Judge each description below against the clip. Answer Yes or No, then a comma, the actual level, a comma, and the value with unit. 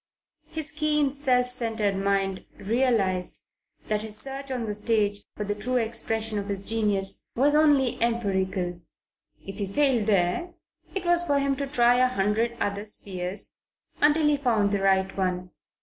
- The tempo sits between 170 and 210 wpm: No, average, 160 wpm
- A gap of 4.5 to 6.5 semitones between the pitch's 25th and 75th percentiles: Yes, average, 5.1 semitones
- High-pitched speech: Yes, high, 220 Hz